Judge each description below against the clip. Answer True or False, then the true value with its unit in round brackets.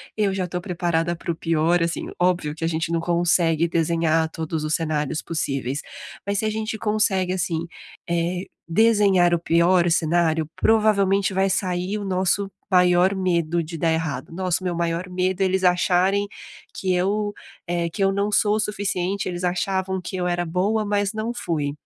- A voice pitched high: False (180 Hz)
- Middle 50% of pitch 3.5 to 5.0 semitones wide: False (2.6 semitones)